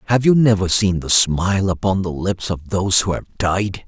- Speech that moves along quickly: Yes, fast, 215 wpm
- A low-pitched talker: Yes, very low, 95 Hz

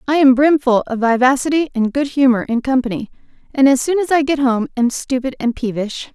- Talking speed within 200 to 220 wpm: Yes, fast, 205 wpm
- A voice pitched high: Yes, very high, 260 Hz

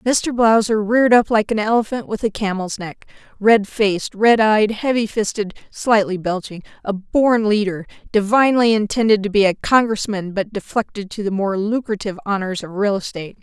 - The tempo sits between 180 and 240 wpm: No, average, 155 wpm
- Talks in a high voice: Yes, high, 210 Hz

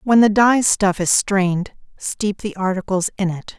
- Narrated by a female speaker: Yes, female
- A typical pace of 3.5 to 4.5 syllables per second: Yes, 4.3 syllables/s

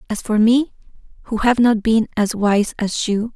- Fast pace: No, average, 195 wpm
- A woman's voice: Yes, female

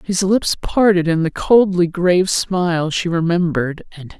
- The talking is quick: No, average, 170 wpm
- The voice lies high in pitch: No, medium, 175 Hz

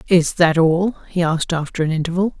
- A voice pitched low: No, medium, 170 Hz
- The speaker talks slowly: No, average, 200 wpm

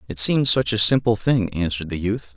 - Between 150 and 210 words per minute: No, fast, 230 wpm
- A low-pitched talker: Yes, low, 105 Hz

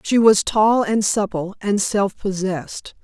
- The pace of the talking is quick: No, average, 160 wpm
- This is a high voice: Yes, high, 205 Hz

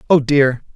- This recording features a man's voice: Yes, male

